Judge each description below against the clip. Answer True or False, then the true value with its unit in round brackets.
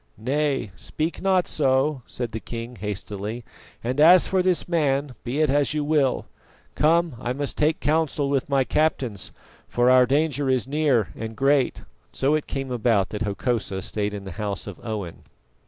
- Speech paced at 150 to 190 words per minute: True (170 wpm)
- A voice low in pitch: True (130 Hz)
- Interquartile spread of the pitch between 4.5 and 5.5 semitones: True (5.0 semitones)